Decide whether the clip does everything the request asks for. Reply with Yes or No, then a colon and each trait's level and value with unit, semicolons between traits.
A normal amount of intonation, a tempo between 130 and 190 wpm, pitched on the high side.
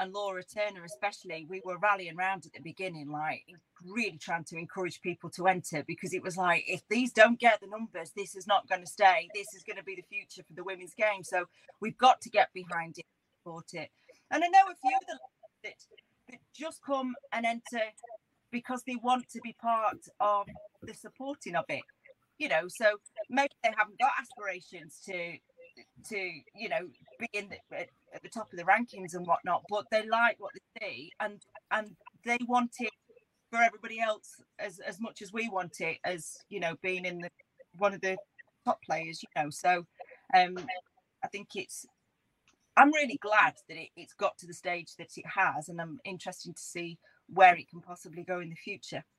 No: average, 4.6 semitones; fast, 205 wpm; high, 200 Hz